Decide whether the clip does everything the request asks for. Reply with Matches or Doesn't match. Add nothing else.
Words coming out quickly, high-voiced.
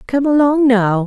Doesn't match